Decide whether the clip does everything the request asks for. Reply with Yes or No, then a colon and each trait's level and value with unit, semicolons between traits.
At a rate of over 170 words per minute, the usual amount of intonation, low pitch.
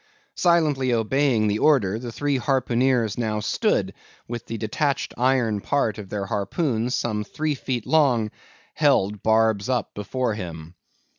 No: average, 140 wpm; average, 4.0 semitones; low, 115 Hz